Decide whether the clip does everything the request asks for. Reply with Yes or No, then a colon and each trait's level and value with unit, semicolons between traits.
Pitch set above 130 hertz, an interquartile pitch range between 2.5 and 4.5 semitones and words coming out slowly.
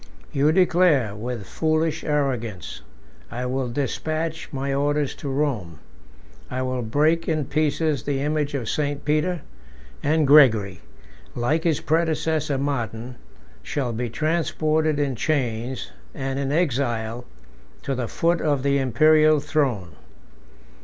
Yes: medium, 140 Hz; average, 3.7 semitones; slow, 125 wpm